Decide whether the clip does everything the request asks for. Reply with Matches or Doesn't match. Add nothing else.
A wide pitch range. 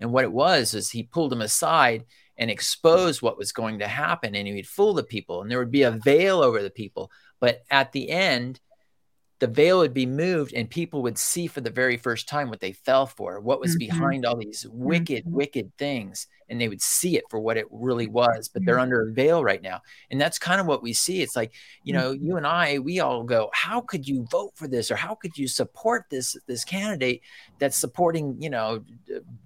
Matches